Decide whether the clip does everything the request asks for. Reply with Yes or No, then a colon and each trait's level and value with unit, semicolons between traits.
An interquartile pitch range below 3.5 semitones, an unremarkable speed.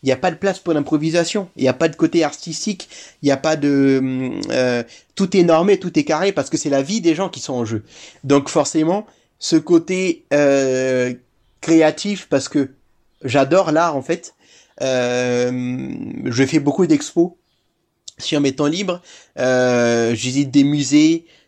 No: average, 4.3 semitones; average, 175 wpm